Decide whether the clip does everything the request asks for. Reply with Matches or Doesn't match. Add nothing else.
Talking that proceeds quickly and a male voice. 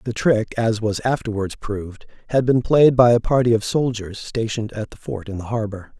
Matches